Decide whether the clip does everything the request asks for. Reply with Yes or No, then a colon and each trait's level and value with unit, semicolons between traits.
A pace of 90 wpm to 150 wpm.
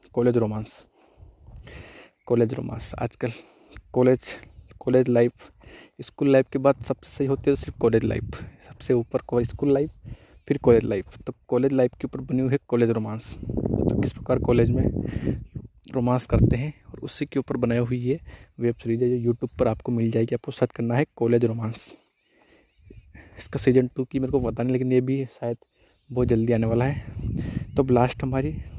No: average, 180 wpm